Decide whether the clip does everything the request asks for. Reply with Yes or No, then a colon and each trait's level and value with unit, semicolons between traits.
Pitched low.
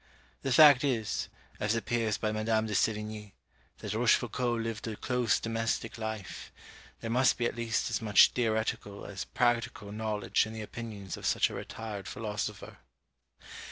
Yes: low, 110 Hz